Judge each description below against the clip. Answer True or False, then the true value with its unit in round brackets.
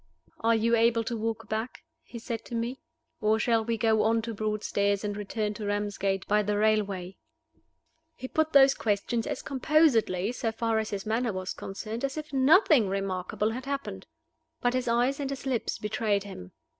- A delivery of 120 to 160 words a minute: False (180 wpm)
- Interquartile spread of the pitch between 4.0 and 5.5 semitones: False (2.9 semitones)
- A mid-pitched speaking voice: False (225 Hz)